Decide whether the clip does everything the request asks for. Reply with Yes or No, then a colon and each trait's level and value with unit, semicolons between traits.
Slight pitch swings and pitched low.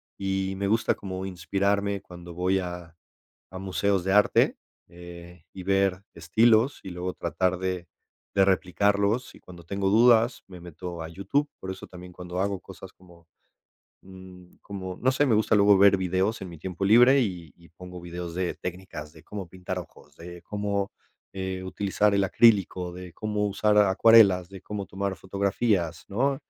Yes: narrow, 2.1 semitones; very low, 95 Hz